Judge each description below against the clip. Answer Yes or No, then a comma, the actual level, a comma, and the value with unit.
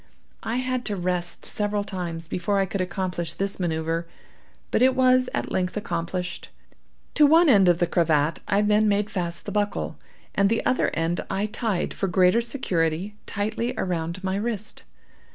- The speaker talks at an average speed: Yes, average, 170 wpm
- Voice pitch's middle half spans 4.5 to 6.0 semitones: No, average, 3.6 semitones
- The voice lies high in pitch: Yes, high, 195 Hz